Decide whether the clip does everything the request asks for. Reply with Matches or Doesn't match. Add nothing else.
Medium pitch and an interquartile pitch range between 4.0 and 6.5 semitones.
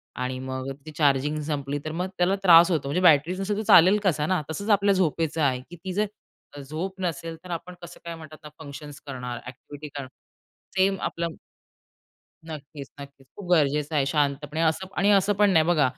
Matches